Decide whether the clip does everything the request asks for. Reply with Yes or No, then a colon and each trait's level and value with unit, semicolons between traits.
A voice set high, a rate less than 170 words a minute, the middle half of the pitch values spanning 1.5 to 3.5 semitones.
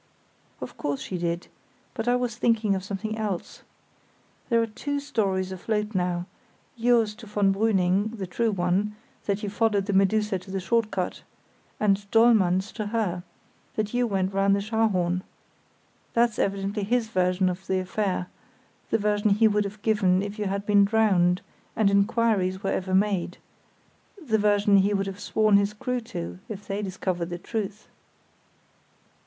Yes: high, 200 Hz; average, 160 wpm; narrow, 2.5 semitones